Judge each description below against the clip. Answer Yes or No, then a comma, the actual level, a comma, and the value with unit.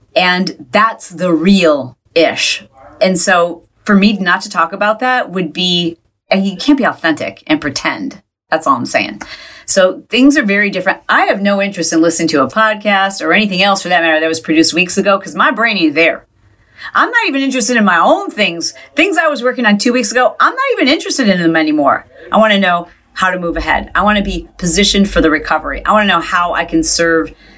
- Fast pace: Yes, fast, 225 wpm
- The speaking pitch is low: No, high, 190 Hz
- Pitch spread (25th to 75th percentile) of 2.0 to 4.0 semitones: No, average, 4.6 semitones